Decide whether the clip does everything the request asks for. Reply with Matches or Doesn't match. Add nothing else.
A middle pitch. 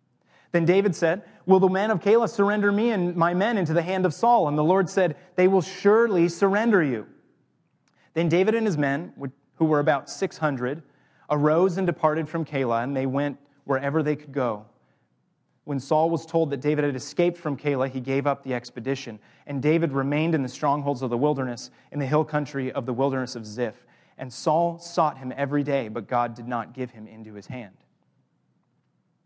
Matches